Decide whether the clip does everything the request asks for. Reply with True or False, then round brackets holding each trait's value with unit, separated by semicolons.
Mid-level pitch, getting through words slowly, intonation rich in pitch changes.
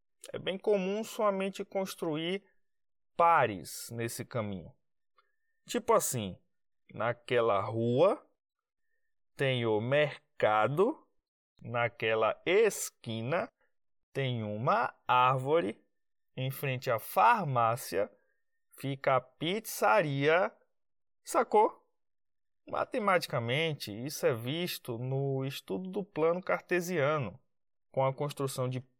True (145 Hz; 85 wpm; 7.9 semitones)